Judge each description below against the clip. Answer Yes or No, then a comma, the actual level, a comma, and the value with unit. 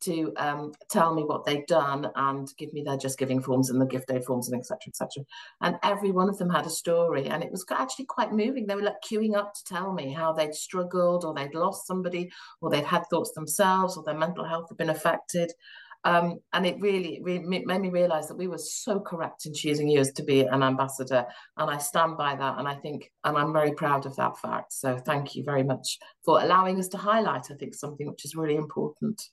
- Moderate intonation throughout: Yes, average, 4.3 semitones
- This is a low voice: No, medium, 160 Hz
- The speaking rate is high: Yes, fast, 240 wpm